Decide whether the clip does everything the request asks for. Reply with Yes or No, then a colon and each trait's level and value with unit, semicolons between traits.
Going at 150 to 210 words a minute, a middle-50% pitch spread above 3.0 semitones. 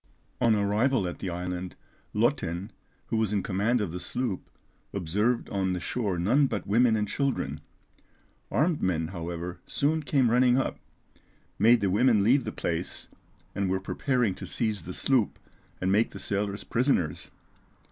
Yes: average, 155 wpm; average, 5.1 semitones